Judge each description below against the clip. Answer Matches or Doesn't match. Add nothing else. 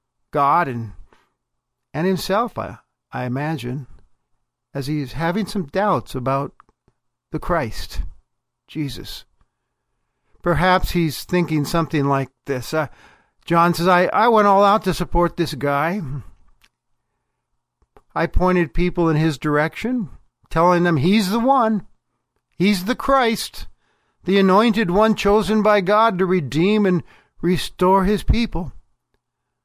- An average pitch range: Doesn't match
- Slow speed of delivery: Matches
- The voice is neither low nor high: Matches